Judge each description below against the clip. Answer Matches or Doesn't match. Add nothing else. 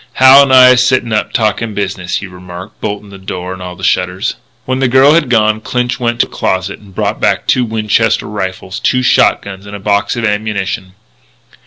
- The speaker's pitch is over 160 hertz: Doesn't match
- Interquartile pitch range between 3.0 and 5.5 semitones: Matches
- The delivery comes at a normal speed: Doesn't match